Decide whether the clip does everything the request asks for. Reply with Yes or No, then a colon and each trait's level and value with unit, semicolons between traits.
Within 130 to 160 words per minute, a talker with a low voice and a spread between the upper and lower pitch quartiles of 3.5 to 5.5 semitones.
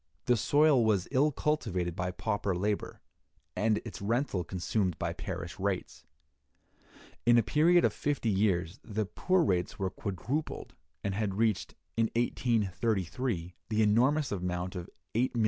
Yes: average, 140 wpm; low, 105 Hz; average, 4.7 semitones